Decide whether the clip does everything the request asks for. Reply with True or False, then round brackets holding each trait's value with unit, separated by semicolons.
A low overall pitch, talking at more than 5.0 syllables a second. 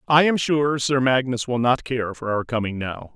False (125 Hz; 4.7 syllables/s)